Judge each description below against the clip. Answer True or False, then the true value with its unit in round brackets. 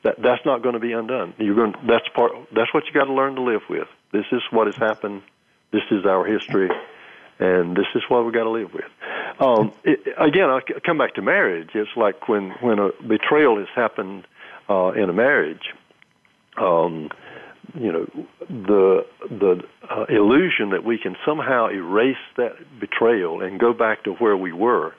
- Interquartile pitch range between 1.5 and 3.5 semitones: False (4.3 semitones)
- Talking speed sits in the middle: True (190 wpm)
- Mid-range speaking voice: False (115 Hz)